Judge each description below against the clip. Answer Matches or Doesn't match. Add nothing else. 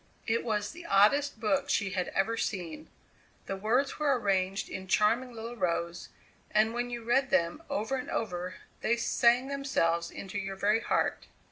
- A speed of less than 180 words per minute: Matches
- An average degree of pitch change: Matches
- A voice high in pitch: Matches